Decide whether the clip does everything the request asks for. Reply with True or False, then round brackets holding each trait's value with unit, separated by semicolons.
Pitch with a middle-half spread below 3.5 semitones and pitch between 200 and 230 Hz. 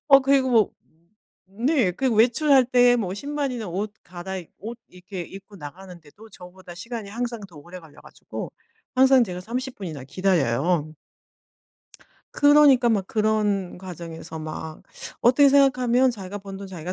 False (5.6 semitones; 205 Hz)